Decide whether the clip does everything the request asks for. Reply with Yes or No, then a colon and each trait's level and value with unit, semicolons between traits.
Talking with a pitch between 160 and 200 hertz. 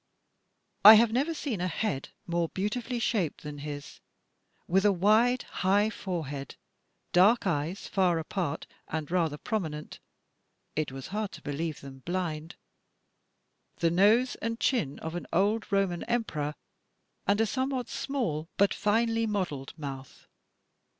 Yes: medium, 185 Hz